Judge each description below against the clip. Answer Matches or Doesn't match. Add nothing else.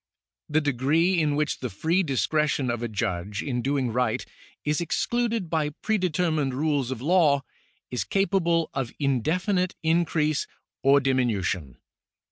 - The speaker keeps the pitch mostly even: Doesn't match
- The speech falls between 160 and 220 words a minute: Doesn't match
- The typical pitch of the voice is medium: Matches